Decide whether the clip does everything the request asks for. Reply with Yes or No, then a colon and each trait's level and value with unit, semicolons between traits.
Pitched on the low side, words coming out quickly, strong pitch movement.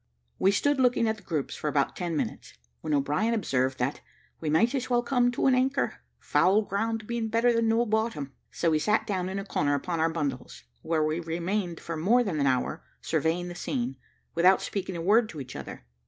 No: medium, 185 Hz; fast, 215 wpm; wide, 6.5 semitones